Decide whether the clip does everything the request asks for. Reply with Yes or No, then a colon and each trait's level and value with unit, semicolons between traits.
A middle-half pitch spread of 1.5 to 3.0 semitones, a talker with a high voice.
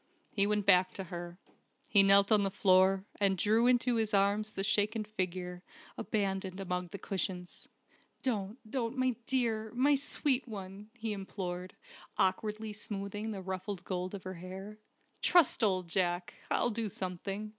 Yes: narrow, 2.6 semitones; high, 200 Hz